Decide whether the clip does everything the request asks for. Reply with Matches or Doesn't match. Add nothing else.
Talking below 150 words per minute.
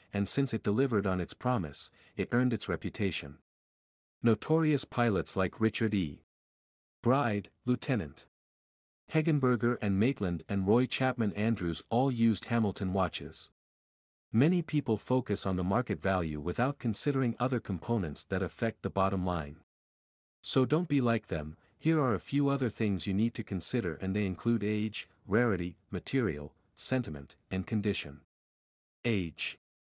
Matches